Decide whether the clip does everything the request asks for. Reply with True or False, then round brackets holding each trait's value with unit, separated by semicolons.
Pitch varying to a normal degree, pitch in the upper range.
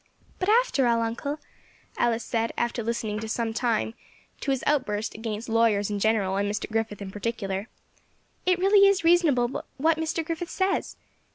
False (6.4 semitones; 235 Hz)